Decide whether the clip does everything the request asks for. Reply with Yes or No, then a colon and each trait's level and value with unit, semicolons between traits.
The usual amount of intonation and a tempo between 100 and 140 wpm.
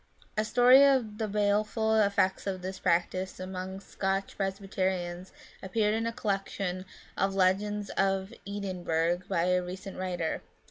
No: narrow, 2.1 semitones; slow, 135 wpm